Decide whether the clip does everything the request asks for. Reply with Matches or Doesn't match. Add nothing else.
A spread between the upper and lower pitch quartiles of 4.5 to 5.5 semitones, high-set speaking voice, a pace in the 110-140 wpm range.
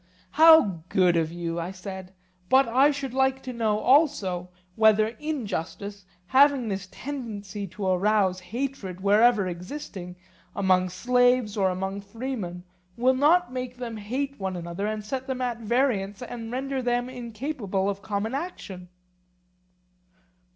Matches